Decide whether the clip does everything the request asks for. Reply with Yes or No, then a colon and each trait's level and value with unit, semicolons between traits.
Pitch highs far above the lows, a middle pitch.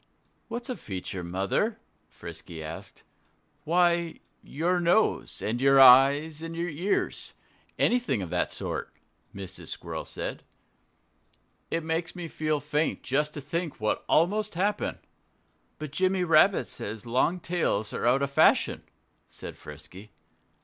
Yes: wide, 7.5 semitones; medium, 150 Hz